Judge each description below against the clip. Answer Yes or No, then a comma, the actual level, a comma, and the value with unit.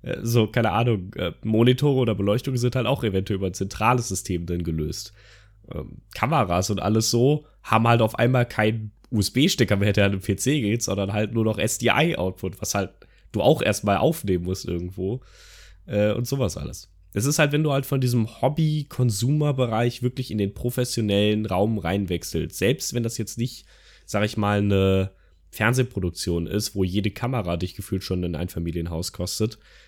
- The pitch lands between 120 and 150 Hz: No, low, 105 Hz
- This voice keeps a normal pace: Yes, average, 175 wpm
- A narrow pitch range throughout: No, average, 4.2 semitones